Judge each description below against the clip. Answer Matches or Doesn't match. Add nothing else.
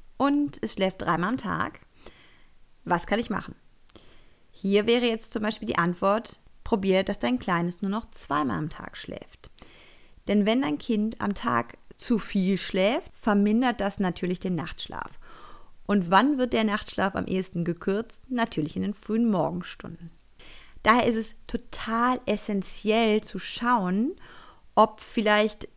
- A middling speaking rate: Matches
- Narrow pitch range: Doesn't match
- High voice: Matches